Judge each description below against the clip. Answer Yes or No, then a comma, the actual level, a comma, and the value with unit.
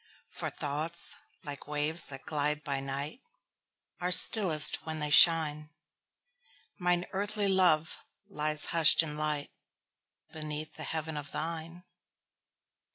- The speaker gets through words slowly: Yes, slow, 100 wpm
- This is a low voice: No, medium, 155 Hz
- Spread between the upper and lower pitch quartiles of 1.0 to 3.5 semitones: Yes, average, 2.7 semitones